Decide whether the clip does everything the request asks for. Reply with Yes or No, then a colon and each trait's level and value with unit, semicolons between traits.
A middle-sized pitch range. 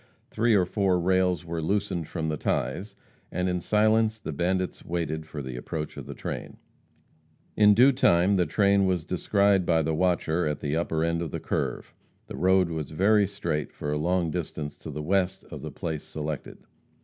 Yes: average, 3.8 semitones